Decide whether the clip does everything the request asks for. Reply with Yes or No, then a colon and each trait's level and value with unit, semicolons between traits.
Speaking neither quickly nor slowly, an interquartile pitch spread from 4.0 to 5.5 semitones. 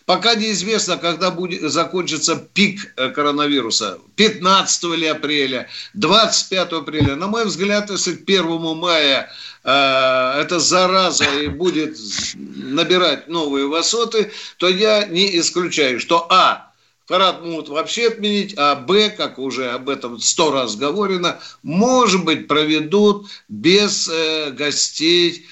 Yes: average, 120 wpm; average, 4.7 semitones